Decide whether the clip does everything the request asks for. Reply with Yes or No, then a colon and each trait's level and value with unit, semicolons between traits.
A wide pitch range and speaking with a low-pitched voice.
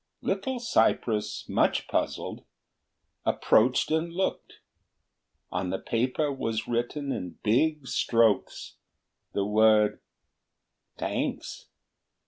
Yes: wide, 6.1 semitones; low, 120 Hz